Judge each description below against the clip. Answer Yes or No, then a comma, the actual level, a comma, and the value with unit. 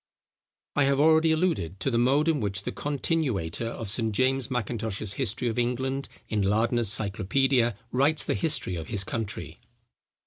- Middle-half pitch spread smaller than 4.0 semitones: No, average, 4.7 semitones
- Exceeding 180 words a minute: No, average, 160 wpm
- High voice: No, low, 120 Hz